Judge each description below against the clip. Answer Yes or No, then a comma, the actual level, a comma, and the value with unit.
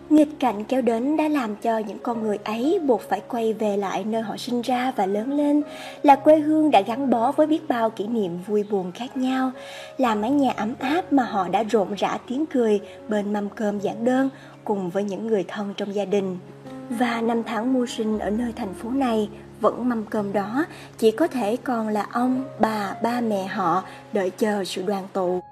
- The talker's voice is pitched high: Yes, high, 225 Hz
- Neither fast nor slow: Yes, average, 215 wpm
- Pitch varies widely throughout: No, average, 4.1 semitones